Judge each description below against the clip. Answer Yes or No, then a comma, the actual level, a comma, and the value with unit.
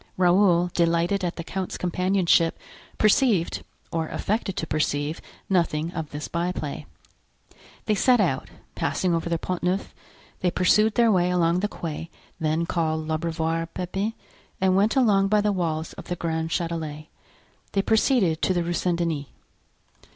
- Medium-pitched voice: Yes, medium, 175 Hz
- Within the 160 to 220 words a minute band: No, average, 150 wpm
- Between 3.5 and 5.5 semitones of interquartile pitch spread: No, average, 2.9 semitones